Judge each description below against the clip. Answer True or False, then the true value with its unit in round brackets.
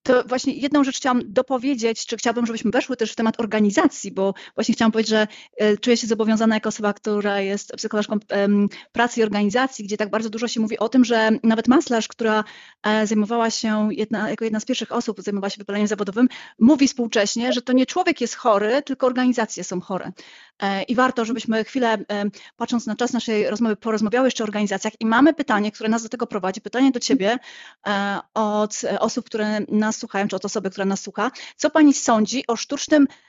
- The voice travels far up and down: False (2.6 semitones)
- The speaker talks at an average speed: False (190 wpm)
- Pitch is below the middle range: False (225 Hz)